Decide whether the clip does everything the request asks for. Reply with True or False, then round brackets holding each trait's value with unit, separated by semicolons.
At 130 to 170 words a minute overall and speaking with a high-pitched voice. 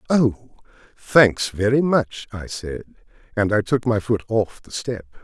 False (160 wpm; 115 Hz)